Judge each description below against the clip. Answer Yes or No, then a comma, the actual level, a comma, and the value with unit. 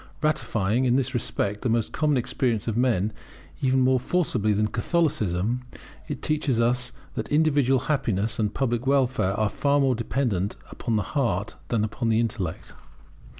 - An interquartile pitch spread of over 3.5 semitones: Yes, average, 3.9 semitones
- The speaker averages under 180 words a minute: Yes, average, 150 wpm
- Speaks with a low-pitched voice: Yes, low, 120 Hz